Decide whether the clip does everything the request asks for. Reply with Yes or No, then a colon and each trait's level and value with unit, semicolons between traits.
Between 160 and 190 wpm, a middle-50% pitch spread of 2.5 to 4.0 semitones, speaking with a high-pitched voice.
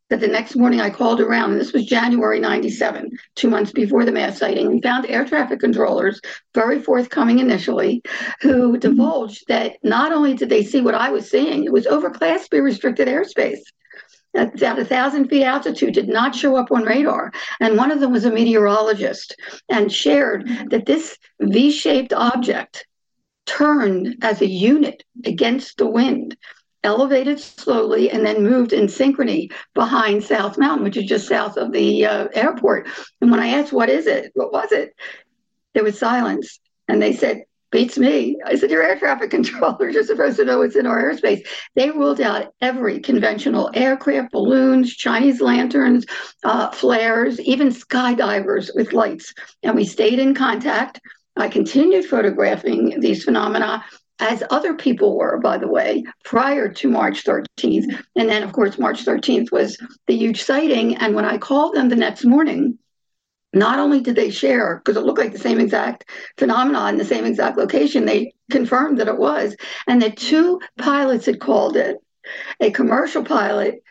Yes: average, 175 wpm; average, 3.7 semitones; very high, 250 Hz